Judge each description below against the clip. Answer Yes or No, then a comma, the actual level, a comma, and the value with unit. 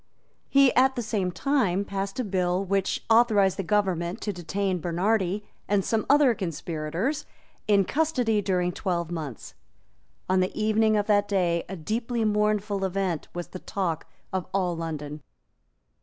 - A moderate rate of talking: Yes, average, 150 wpm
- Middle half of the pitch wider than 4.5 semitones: No, average, 3.5 semitones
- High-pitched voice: Yes, high, 195 Hz